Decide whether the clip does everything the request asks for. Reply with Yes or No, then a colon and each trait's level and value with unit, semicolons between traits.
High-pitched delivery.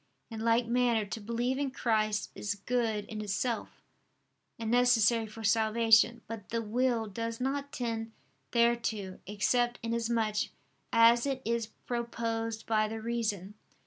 Yes: high, 230 Hz